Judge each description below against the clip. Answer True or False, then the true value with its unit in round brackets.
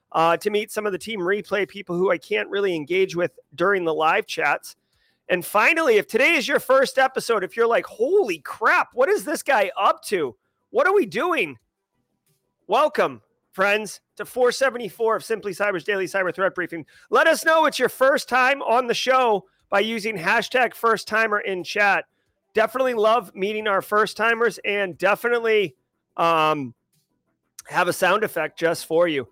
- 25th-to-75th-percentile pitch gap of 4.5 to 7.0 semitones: True (4.8 semitones)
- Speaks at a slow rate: False (175 wpm)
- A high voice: True (210 Hz)